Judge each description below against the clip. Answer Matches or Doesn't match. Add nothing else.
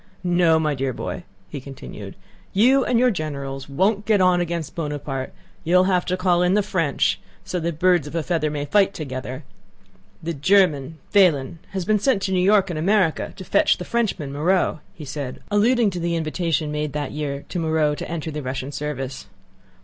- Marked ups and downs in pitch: Doesn't match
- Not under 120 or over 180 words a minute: Doesn't match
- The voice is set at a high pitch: Doesn't match